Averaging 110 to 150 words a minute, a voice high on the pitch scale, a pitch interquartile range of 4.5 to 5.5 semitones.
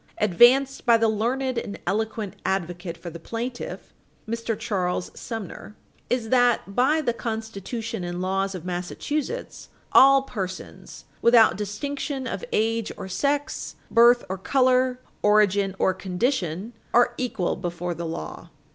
Yes: slow, 135 wpm; high, 220 Hz; average, 4.8 semitones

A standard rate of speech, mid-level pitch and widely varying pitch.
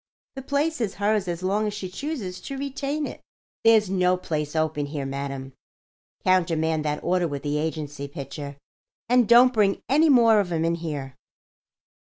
Yes: average, 170 wpm; medium, 180 Hz; wide, 7.1 semitones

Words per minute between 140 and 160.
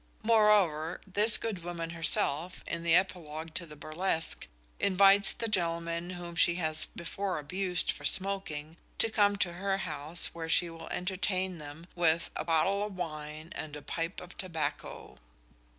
Yes: average, 155 wpm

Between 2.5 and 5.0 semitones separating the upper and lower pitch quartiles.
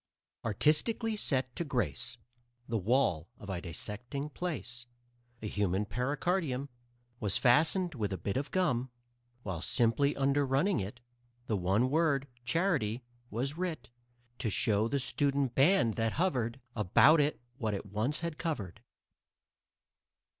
No: wide, 5.6 semitones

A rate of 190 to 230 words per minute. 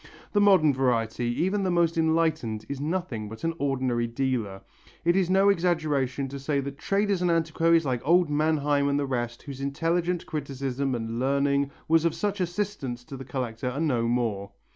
No: average, 180 wpm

